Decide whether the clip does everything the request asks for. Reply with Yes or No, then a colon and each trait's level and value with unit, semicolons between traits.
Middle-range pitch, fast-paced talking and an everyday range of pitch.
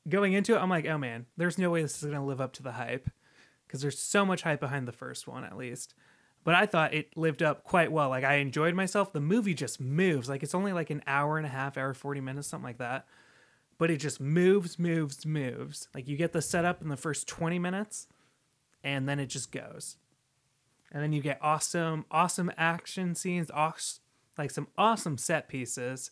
Yes: medium, 150 Hz; fast, 220 wpm; average, 3.7 semitones